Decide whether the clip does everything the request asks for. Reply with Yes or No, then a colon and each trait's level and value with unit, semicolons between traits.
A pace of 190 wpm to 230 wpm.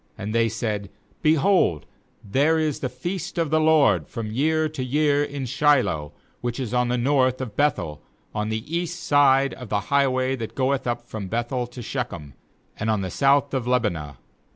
Yes: average, 195 wpm